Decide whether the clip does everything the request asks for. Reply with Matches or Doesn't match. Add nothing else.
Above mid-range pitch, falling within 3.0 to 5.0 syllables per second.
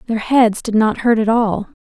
Matches